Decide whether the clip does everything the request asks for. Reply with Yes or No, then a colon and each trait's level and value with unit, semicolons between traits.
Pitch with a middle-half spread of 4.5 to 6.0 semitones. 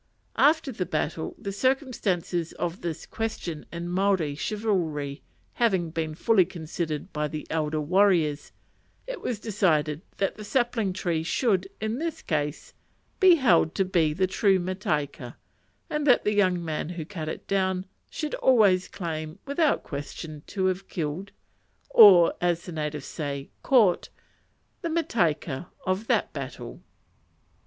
Yes: average, 5.0 semitones